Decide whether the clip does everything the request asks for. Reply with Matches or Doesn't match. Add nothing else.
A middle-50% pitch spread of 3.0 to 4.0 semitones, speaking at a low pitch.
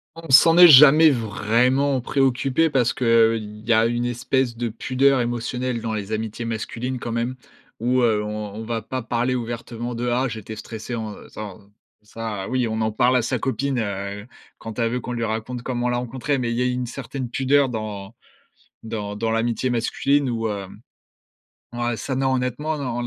Doesn't match